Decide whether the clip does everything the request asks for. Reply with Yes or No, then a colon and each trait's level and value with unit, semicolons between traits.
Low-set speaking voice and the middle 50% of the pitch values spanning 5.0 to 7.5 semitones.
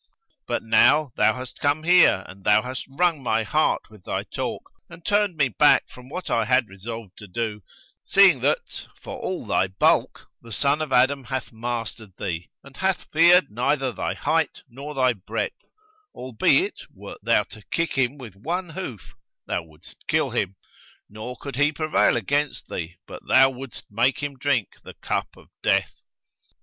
Yes: low, 130 Hz; average, 5.3 semitones